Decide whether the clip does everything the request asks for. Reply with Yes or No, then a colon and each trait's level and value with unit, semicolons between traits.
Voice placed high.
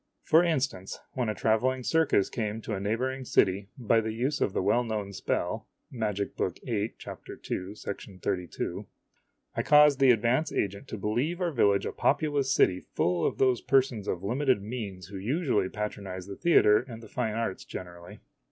No: low, 110 Hz